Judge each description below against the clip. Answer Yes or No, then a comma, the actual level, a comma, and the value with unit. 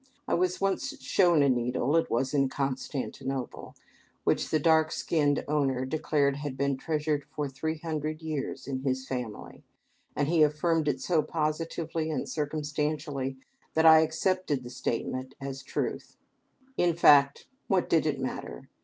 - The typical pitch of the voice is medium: Yes, medium, 150 Hz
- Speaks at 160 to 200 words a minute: No, average, 150 wpm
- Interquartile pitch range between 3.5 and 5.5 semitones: No, average, 2.9 semitones